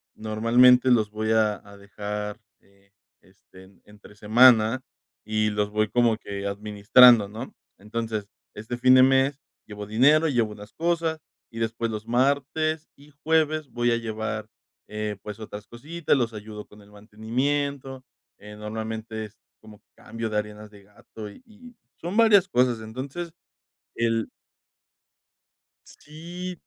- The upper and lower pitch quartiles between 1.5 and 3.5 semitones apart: No, average, 4.0 semitones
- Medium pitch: No, low, 110 Hz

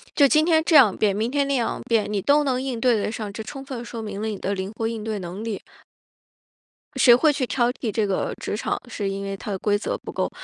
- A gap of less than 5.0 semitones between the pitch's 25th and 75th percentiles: Yes, average, 4.1 semitones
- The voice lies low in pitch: No, high, 225 Hz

